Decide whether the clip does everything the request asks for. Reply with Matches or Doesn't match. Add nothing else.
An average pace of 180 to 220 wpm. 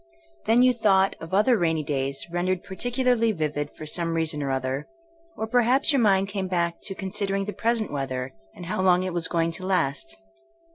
Matches